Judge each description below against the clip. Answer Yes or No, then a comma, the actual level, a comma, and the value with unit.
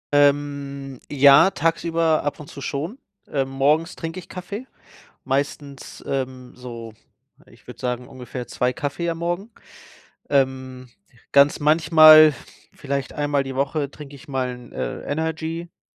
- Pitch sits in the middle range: Yes, medium, 145 Hz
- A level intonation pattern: No, average, 3.2 semitones